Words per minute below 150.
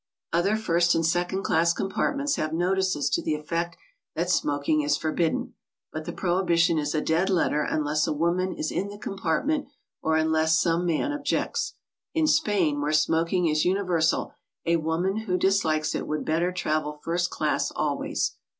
No: average, 170 wpm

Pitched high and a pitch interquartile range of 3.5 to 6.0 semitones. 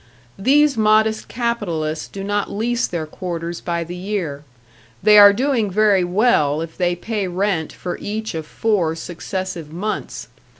Yes: high, 195 Hz; average, 4.2 semitones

